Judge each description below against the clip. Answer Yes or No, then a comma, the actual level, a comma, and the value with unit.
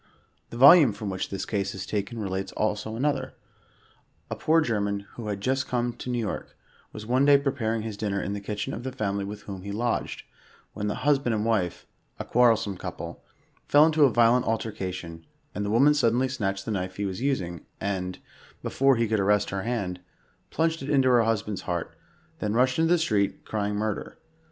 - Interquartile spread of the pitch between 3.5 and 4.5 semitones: Yes, average, 4.1 semitones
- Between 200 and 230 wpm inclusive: Yes, fast, 205 wpm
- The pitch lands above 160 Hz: No, low, 110 Hz